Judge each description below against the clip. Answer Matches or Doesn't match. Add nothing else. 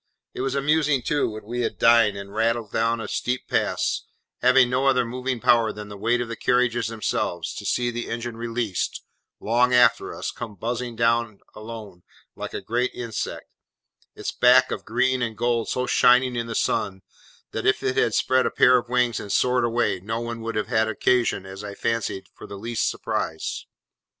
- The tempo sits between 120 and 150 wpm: Doesn't match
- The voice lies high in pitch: Doesn't match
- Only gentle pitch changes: Matches